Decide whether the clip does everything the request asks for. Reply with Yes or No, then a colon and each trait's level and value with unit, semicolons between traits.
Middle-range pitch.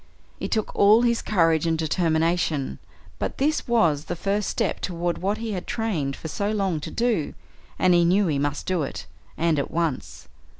Yes: medium, 175 Hz